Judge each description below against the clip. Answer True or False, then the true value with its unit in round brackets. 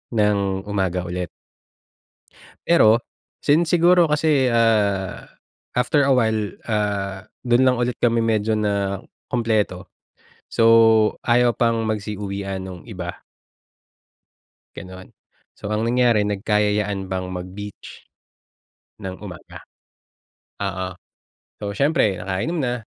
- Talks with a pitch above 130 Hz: False (105 Hz)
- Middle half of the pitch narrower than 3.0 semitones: False (3.5 semitones)